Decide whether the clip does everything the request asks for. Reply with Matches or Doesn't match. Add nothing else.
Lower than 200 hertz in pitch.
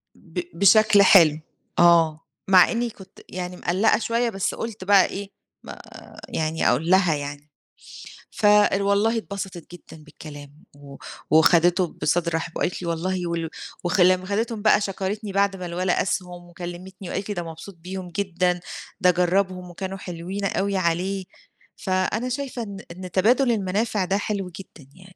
Matches